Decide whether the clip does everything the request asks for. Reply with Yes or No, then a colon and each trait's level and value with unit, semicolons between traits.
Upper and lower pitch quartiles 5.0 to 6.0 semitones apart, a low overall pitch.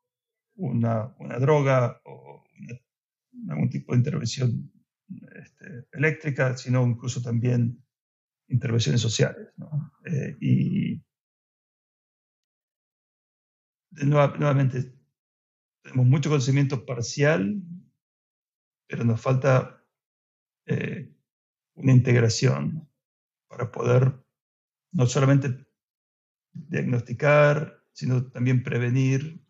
No: average, 3.2 semitones; low, 130 Hz